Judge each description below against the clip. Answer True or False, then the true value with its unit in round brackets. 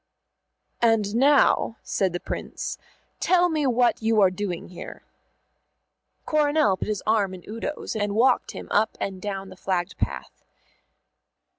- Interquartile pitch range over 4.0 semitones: True (4.6 semitones)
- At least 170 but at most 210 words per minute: False (140 wpm)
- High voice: True (215 Hz)